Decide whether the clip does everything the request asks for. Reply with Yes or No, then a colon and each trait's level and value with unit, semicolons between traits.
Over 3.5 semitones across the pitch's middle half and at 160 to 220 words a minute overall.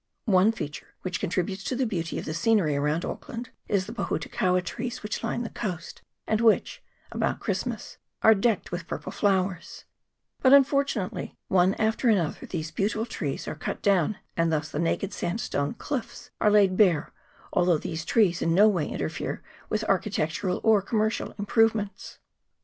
Yes: average, 4.4 semitones; average, 165 wpm